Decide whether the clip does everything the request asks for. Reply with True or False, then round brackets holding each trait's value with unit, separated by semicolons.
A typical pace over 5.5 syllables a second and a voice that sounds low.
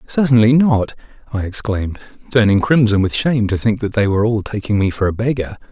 True (6.1 syllables/s; 110 Hz)